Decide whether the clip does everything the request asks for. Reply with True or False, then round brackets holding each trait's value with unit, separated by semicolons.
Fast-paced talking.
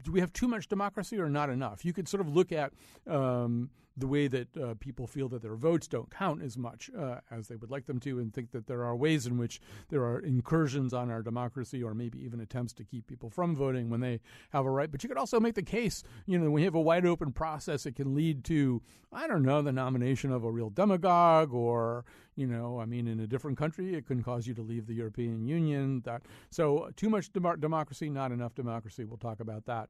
True (245 wpm)